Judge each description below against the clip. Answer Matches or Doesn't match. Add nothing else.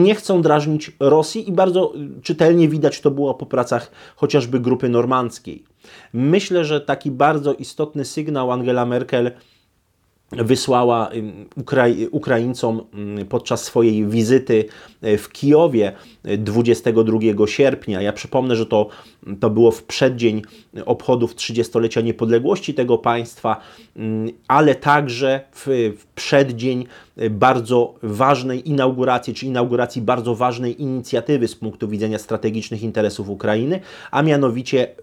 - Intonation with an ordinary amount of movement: Matches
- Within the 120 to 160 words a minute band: Doesn't match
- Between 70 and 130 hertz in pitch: Matches